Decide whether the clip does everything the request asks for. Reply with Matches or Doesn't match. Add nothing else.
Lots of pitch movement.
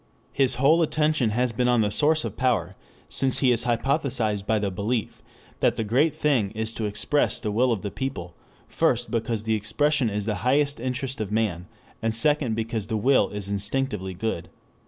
Doesn't match